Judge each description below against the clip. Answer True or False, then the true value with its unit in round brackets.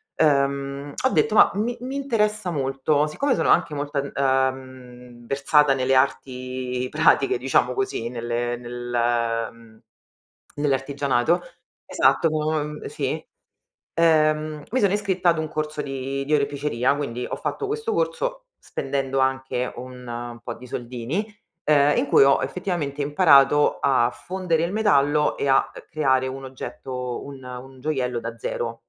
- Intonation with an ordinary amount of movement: True (3.6 semitones)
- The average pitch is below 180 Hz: True (140 Hz)